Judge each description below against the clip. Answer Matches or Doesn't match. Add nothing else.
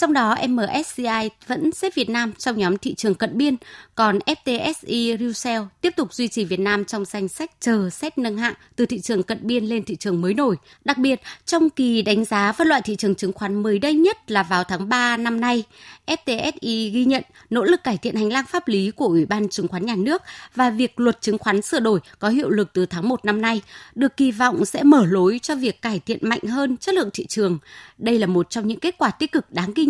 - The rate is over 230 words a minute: Matches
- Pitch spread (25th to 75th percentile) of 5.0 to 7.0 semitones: Doesn't match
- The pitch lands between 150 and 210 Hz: Doesn't match